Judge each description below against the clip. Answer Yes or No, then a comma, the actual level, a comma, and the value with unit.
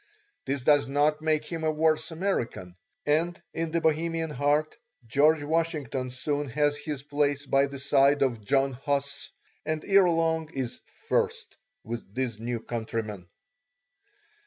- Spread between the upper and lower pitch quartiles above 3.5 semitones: No, average, 3.0 semitones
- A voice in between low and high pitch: Yes, medium, 145 Hz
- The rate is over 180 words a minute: No, average, 140 wpm